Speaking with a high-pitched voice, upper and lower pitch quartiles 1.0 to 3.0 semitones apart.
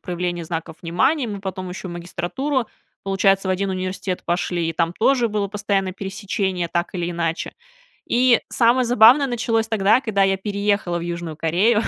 No: high, 195 Hz; average, 4.0 semitones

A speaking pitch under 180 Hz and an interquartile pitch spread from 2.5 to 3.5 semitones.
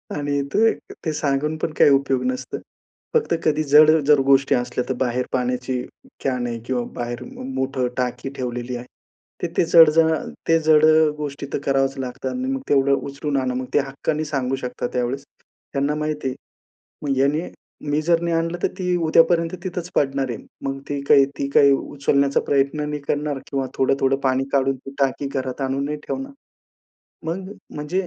Yes: medium, 140 Hz; average, 2.8 semitones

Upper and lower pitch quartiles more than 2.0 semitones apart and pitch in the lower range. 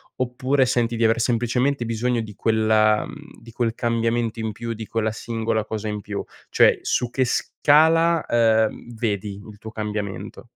No: narrow, 1.7 semitones; low, 115 Hz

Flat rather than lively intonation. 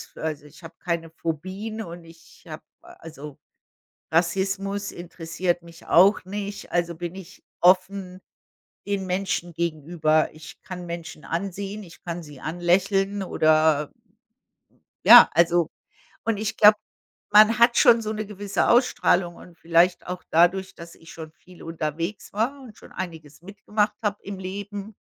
No: average, 3.3 semitones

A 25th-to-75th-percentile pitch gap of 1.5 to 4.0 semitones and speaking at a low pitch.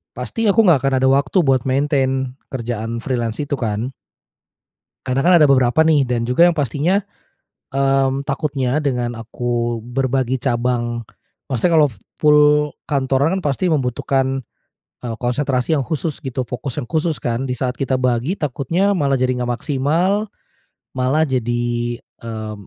Yes: average, 3.3 semitones; low, 130 Hz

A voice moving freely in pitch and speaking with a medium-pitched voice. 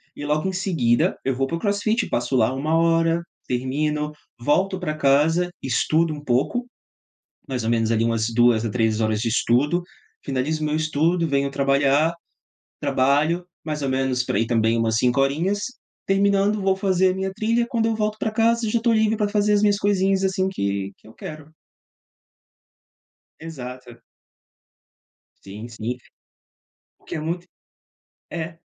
Yes: wide, 7.2 semitones; medium, 155 Hz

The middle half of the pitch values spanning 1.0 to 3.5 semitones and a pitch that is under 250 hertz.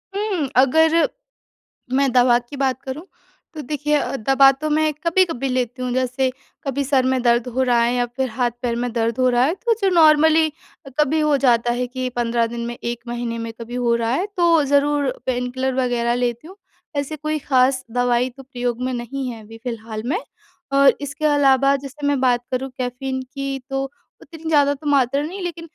No: average, 3.1 semitones; very high, 260 Hz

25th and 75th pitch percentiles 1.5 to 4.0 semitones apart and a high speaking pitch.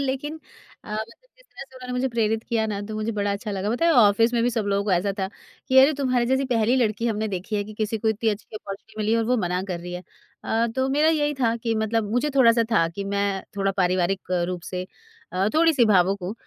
Yes: average, 3.6 semitones; high, 220 Hz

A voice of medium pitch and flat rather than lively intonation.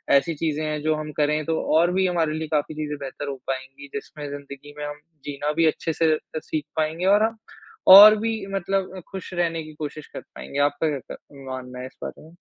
Yes: medium, 155 Hz; narrow, 2.3 semitones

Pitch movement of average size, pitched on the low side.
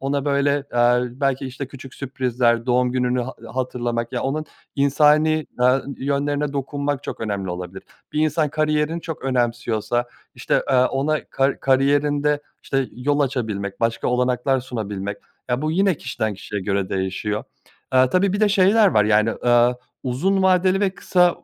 Yes: average, 3.6 semitones; low, 130 Hz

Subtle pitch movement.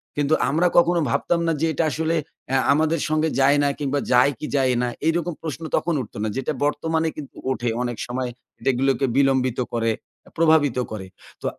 No: average, 3.9 semitones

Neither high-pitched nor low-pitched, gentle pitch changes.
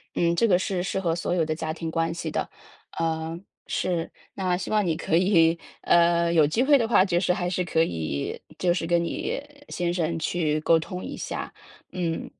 Yes: medium, 170 Hz; narrow, 1.8 semitones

